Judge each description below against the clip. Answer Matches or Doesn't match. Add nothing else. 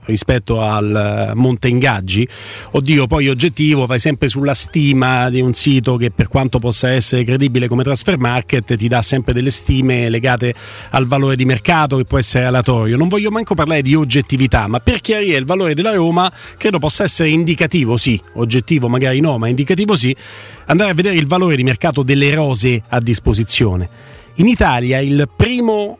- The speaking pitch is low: Matches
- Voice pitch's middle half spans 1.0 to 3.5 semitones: Doesn't match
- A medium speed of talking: Doesn't match